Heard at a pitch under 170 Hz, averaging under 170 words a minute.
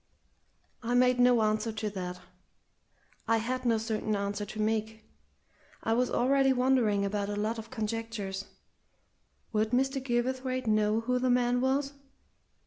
No: high, 225 Hz; average, 140 wpm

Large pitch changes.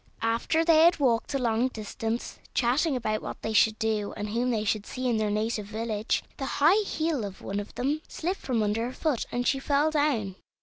No: average, 4.7 semitones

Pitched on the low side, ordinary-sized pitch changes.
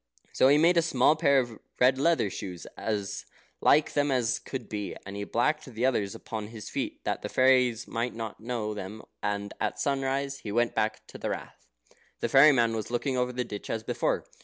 Yes: low, 120 Hz; average, 3.9 semitones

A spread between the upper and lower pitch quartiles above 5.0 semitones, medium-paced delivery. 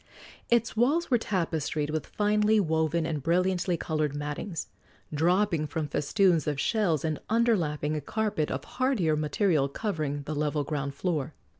Yes: wide, 5.5 semitones; average, 145 wpm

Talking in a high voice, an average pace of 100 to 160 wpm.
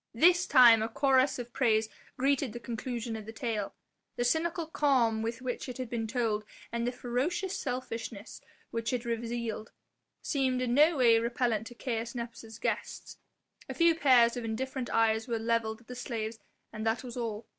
No: high, 235 Hz; average, 175 wpm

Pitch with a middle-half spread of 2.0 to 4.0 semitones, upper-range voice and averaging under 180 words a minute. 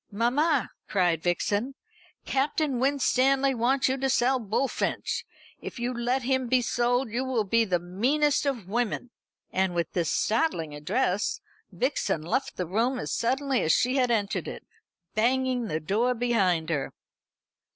No: average, 5.1 semitones; high, 240 Hz; average, 150 wpm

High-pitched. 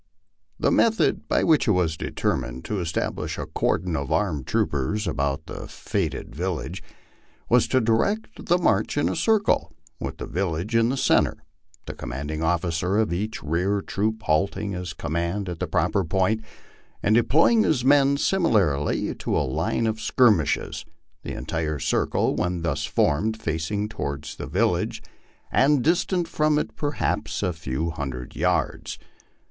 No: very low, 95 Hz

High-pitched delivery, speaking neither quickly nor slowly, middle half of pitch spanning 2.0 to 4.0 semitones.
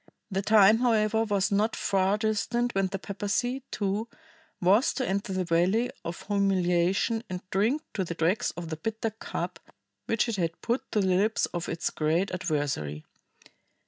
Yes: high, 195 Hz; average, 160 wpm; average, 3.6 semitones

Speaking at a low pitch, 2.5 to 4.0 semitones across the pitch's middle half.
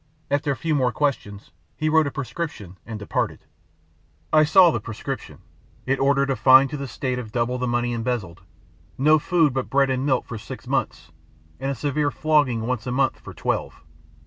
Yes: low, 130 Hz; average, 3.3 semitones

